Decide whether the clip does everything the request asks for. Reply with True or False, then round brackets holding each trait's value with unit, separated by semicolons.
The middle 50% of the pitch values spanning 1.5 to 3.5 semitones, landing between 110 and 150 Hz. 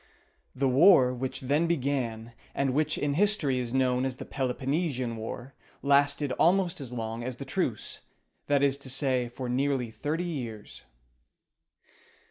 True (2.5 semitones; 135 Hz)